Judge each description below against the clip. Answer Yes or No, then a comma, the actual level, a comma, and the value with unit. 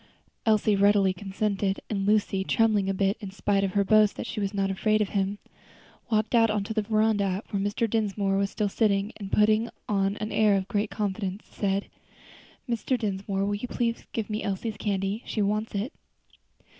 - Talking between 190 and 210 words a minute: Yes, average, 195 wpm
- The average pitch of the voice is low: No, high, 205 Hz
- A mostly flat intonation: Yes, narrow, 1.6 semitones